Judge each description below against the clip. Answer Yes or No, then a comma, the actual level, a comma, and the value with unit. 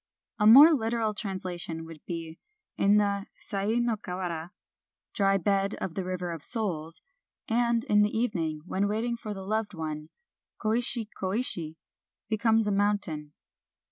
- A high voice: Yes, high, 200 Hz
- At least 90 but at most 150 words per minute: No, average, 160 wpm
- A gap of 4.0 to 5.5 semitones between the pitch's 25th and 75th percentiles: Yes, average, 4.3 semitones